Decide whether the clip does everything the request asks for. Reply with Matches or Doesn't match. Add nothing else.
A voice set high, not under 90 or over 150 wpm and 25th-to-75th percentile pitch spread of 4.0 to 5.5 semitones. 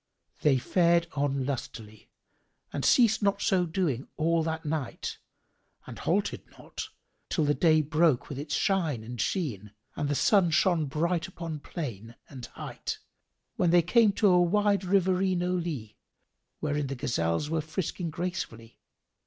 Doesn't match